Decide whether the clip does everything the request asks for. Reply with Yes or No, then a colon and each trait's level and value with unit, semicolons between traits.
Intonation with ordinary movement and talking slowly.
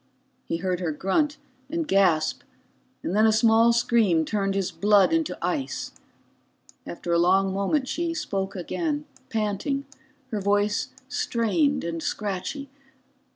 No: wide, 6.6 semitones; slow, 130 wpm